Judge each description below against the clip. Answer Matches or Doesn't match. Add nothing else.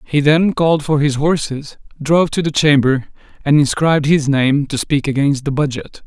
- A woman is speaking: Doesn't match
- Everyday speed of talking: Matches